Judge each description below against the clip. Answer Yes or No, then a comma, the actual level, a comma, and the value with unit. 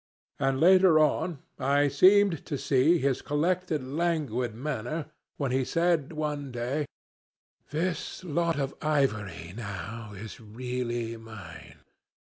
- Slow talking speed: Yes, slow, 115 wpm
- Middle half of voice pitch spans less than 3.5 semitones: No, average, 5.0 semitones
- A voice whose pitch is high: No, medium, 140 Hz